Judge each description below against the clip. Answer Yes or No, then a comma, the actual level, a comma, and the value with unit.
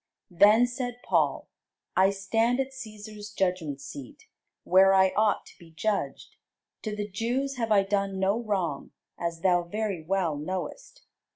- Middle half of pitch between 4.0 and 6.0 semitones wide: No, average, 3.5 semitones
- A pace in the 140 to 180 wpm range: Yes, average, 150 wpm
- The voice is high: Yes, high, 200 Hz